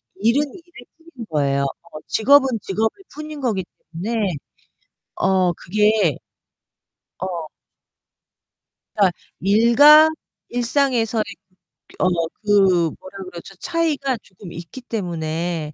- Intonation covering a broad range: Yes, wide, 6.2 semitones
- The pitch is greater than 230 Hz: No, high, 210 Hz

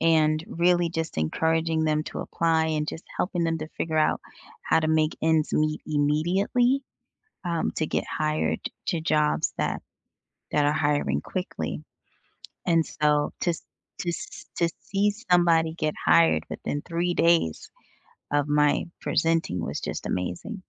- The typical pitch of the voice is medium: Yes, medium, 160 Hz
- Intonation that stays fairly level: Yes, narrow, 1.9 semitones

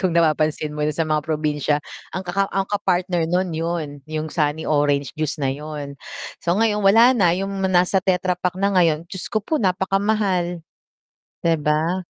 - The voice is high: No, medium, 170 Hz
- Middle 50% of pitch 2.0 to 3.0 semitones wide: No, average, 3.7 semitones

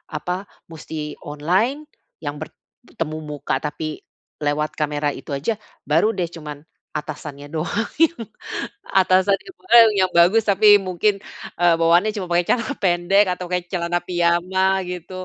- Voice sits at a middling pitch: Yes, medium, 175 Hz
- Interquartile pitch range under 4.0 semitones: Yes, average, 3.6 semitones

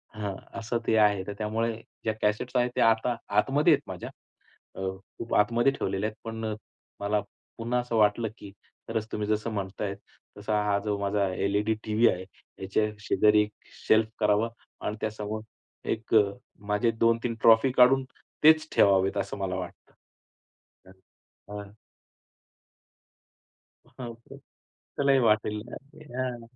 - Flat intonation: Yes, narrow, 2.1 semitones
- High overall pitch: No, low, 110 Hz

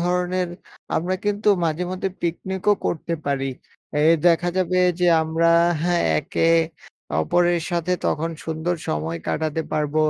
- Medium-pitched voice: Yes, medium, 170 Hz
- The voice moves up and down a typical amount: No, narrow, 2.1 semitones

